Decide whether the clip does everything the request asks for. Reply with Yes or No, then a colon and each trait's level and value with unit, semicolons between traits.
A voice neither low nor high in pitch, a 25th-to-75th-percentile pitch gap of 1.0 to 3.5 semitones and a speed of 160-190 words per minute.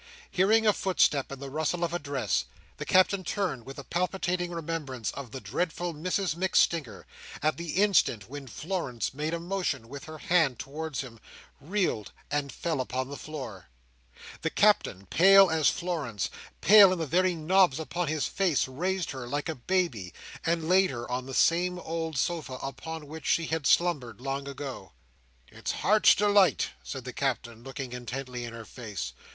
No: medium, 155 Hz; average, 5.3 semitones; average, 170 wpm